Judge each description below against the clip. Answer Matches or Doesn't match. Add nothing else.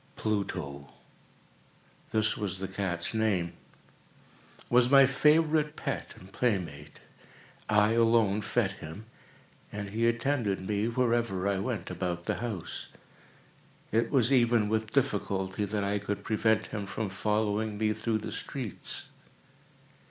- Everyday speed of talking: Doesn't match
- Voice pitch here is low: Matches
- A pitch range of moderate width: Matches